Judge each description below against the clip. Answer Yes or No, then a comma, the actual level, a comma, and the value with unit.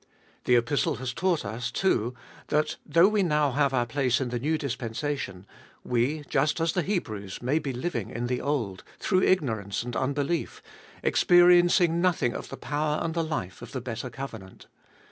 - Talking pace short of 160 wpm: No, average, 180 wpm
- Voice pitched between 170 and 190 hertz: No, medium, 140 Hz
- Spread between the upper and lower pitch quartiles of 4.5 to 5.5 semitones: Yes, average, 5.0 semitones